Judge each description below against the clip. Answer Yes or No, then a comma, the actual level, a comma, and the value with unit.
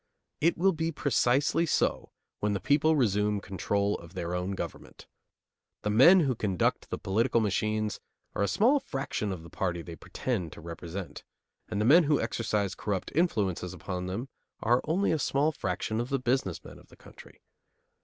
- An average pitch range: No, wide, 6.8 semitones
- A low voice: Yes, low, 105 Hz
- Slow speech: No, average, 175 wpm